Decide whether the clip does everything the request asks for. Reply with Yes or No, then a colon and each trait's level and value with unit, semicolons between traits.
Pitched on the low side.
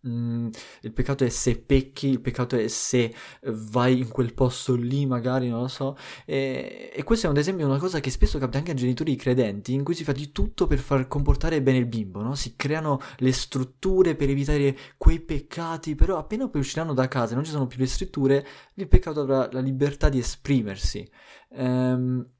Yes: low, 130 Hz